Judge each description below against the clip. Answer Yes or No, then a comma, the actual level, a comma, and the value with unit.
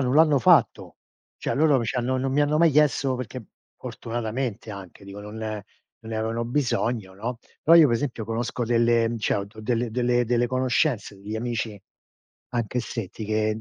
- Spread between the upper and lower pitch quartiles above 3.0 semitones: No, average, 2.7 semitones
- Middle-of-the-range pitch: No, low, 120 Hz